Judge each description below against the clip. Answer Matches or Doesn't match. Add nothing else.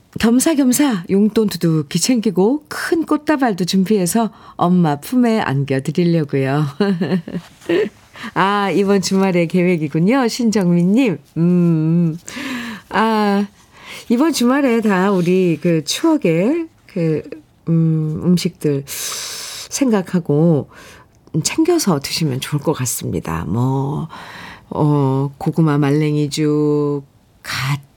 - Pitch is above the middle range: Doesn't match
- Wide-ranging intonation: Matches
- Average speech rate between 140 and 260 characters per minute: Matches